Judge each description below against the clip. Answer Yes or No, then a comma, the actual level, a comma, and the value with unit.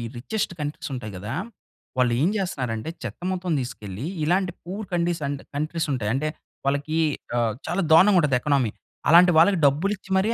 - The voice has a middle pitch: Yes, medium, 150 Hz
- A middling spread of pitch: No, wide, 6.1 semitones